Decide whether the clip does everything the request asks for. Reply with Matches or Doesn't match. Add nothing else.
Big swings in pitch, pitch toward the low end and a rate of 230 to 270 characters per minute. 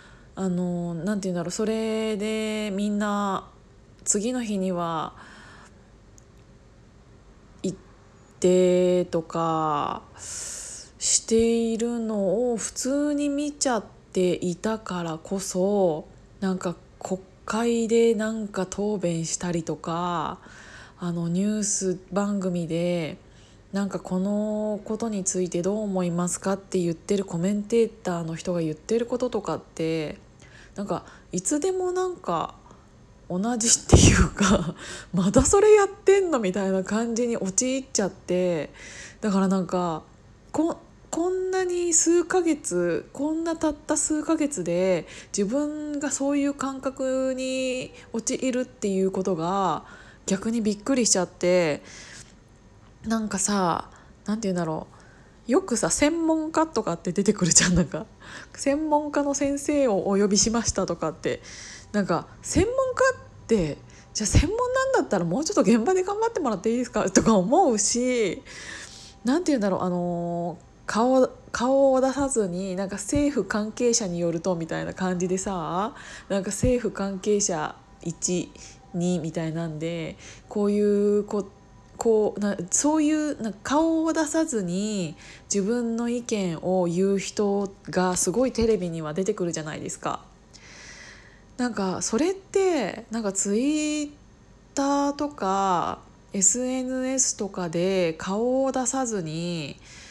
Doesn't match